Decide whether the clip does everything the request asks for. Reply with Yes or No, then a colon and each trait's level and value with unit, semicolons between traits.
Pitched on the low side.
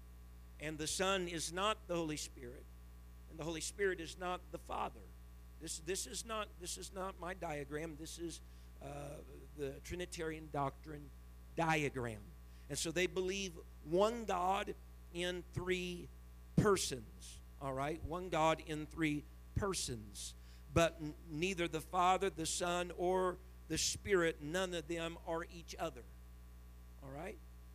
No: medium, 155 Hz